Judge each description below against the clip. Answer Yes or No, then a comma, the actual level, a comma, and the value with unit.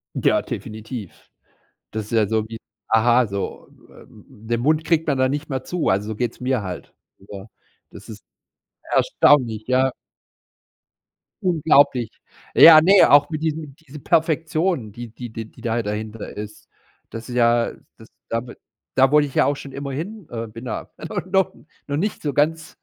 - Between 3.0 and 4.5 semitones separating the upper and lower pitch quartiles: No, average, 5.2 semitones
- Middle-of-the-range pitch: No, low, 130 Hz